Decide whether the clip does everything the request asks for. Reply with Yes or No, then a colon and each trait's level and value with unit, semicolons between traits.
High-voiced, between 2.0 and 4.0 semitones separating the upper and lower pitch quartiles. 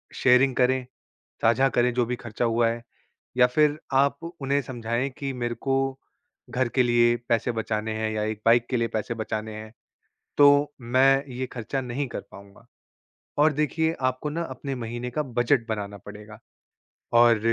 No: low, 120 Hz; average, 3.0 semitones